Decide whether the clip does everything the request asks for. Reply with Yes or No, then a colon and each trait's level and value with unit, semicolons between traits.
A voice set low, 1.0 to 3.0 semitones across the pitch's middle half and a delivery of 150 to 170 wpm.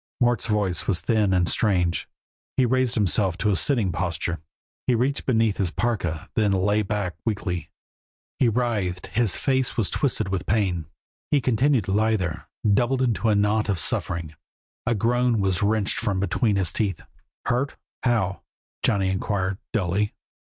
No: low, 105 Hz; average, 3.9 semitones; average, 160 wpm